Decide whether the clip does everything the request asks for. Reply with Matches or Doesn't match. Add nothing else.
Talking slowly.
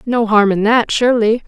Doesn't match